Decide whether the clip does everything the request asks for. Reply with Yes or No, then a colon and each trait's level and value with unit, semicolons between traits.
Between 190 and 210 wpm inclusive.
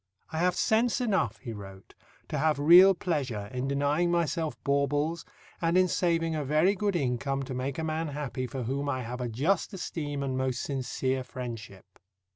No: average, 180 wpm